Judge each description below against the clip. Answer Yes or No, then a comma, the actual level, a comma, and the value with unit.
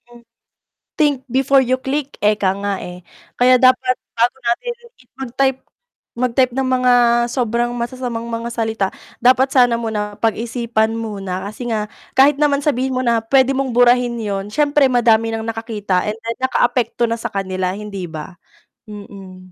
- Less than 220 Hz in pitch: No, high, 235 Hz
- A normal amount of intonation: Yes, average, 3.4 semitones